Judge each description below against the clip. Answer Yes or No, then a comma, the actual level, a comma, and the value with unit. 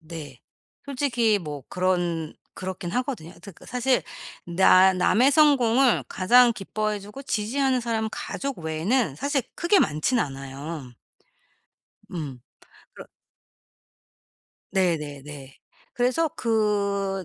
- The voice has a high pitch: Yes, high, 200 Hz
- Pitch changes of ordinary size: No, wide, 7.3 semitones